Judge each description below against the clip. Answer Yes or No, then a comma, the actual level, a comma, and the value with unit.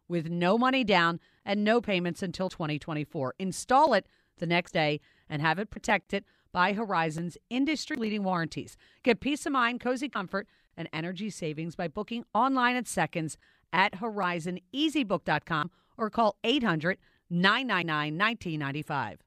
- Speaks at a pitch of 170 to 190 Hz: Yes, medium, 185 Hz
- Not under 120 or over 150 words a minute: Yes, slow, 135 wpm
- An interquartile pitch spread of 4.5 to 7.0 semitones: Yes, average, 4.9 semitones